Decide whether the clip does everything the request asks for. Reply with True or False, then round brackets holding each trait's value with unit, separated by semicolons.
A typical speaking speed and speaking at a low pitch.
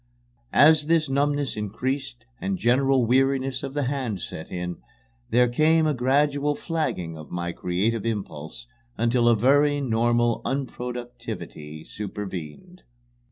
False (120 wpm; 125 Hz)